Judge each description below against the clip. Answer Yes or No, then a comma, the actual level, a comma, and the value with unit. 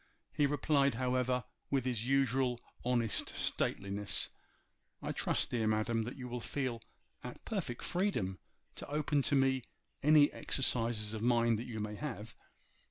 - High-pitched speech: No, low, 125 Hz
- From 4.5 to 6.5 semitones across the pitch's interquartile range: No, average, 3.3 semitones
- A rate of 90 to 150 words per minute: Yes, average, 145 wpm